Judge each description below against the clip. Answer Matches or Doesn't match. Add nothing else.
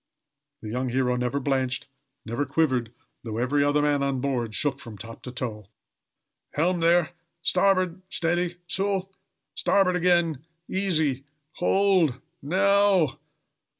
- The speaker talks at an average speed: Doesn't match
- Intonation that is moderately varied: Doesn't match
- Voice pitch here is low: Doesn't match